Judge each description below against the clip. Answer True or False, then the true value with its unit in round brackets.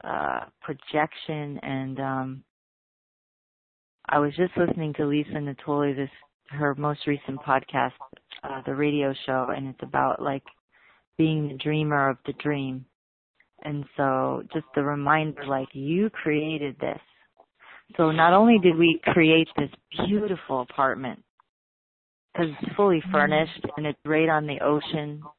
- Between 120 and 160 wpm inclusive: True (135 wpm)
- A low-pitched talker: False (150 Hz)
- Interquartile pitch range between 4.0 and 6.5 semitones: False (2.4 semitones)